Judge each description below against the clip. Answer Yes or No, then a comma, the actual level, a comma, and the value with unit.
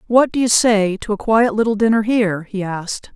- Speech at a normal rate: No, fast, 230 wpm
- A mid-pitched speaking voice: No, high, 215 Hz